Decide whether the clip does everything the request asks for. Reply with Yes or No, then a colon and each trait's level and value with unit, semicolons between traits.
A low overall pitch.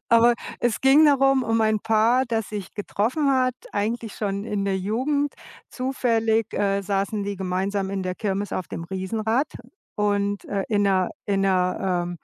No: high, 210 Hz